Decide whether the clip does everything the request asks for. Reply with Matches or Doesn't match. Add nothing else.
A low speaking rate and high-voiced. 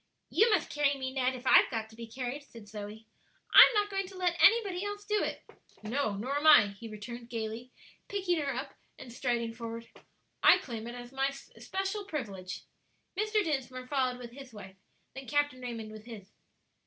Doesn't match